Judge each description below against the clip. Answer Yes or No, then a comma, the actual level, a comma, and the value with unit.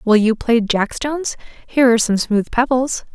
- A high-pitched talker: Yes, high, 240 Hz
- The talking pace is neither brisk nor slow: Yes, average, 190 wpm